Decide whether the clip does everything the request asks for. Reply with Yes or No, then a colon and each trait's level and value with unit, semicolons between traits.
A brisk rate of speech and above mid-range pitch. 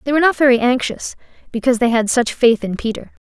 Yes: fast, 220 wpm; high, 245 Hz